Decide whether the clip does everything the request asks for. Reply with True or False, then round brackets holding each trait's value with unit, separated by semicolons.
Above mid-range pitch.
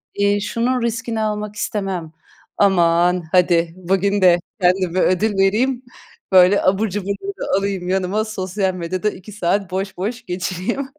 True (195 Hz)